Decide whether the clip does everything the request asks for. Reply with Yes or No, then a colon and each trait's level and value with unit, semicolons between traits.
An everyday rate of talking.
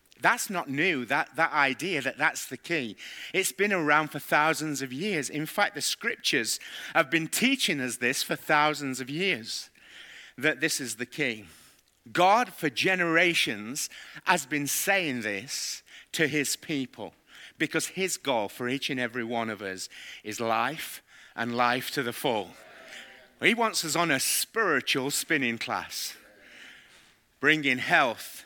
Yes: average, 150 wpm